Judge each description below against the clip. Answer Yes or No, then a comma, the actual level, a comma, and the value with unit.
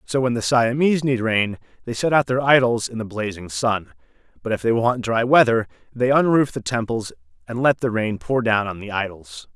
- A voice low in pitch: Yes, low, 115 Hz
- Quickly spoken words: Yes, fast, 215 wpm